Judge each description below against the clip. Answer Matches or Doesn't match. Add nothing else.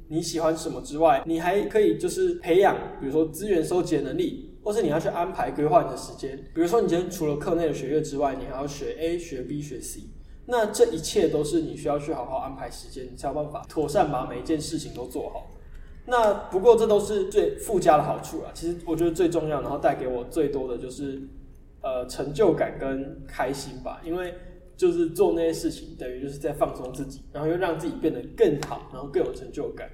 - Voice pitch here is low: Doesn't match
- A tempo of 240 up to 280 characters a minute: Doesn't match